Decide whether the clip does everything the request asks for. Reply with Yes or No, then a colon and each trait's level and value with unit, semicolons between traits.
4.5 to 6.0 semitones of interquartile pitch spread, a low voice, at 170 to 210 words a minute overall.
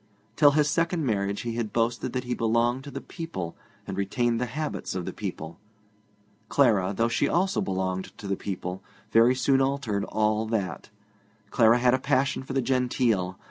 Yes: average, 4.9 semitones; low, 115 Hz; average, 180 wpm